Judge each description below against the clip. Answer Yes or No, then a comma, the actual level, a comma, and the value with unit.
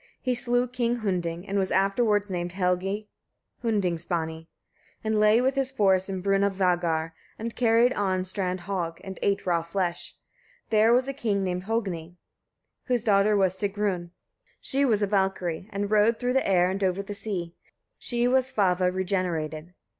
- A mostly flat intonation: No, average, 3.3 semitones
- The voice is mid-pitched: No, high, 195 Hz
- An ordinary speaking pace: Yes, average, 160 wpm